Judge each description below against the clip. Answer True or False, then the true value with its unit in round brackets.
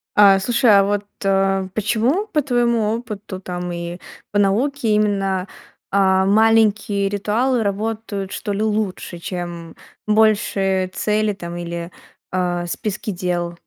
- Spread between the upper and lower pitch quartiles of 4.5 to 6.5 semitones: False (2.7 semitones)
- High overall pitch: True (200 Hz)